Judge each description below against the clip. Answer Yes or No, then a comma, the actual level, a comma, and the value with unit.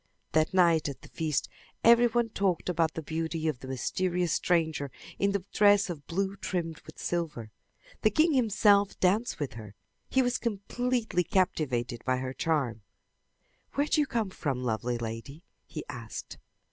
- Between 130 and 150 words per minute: No, average, 160 wpm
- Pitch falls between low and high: Yes, medium, 170 Hz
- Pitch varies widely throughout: Yes, wide, 6.7 semitones